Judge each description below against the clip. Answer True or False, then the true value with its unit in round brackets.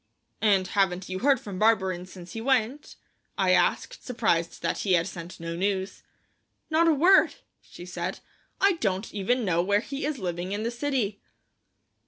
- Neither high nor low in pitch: False (200 Hz)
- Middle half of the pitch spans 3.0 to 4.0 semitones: False (5.4 semitones)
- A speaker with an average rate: True (170 wpm)